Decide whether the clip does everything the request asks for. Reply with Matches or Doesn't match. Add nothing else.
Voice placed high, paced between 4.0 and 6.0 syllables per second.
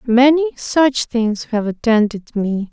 Doesn't match